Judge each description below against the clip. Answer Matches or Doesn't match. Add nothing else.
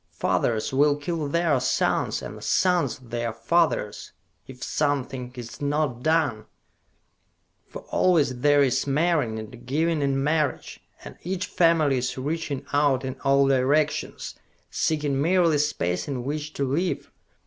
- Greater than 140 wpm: Doesn't match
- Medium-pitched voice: Matches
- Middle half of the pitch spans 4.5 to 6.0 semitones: Doesn't match